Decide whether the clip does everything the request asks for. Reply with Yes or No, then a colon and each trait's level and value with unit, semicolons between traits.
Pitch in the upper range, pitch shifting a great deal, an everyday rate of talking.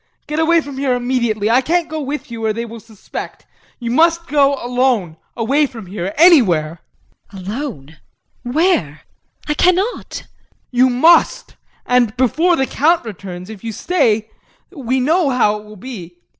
Yes: very high, 250 Hz; wide, 5.9 semitones; average, 160 wpm